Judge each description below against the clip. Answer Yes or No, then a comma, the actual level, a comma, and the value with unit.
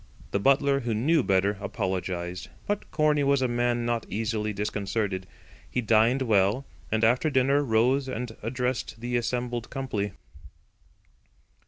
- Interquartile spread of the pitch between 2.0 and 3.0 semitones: No, average, 3.8 semitones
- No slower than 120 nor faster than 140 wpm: Yes, slow, 135 wpm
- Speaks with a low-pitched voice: Yes, low, 120 Hz